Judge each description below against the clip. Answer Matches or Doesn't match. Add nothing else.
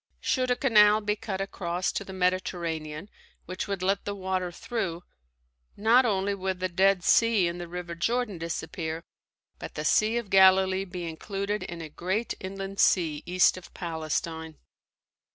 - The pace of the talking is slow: Doesn't match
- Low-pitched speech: Doesn't match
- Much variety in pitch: Doesn't match